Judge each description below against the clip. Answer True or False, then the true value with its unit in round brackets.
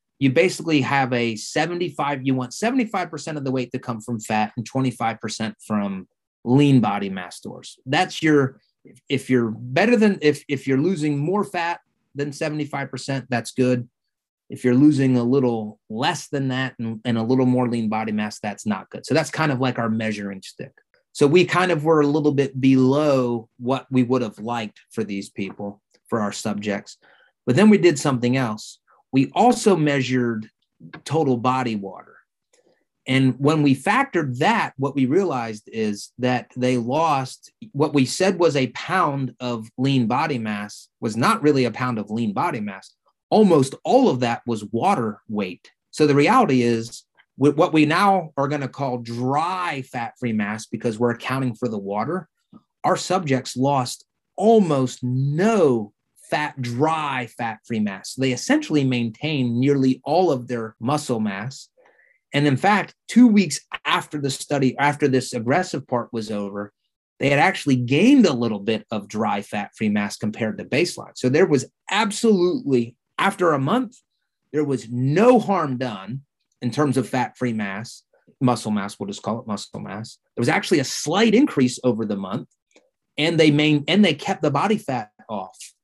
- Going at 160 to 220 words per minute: True (175 wpm)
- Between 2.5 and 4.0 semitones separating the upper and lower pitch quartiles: False (4.4 semitones)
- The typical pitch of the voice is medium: False (130 Hz)